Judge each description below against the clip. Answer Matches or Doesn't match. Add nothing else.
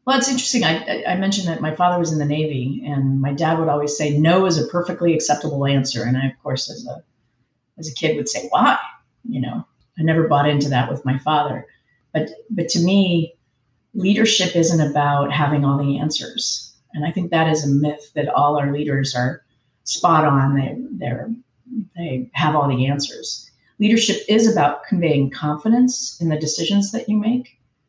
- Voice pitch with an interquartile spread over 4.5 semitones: Doesn't match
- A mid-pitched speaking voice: Matches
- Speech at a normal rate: Matches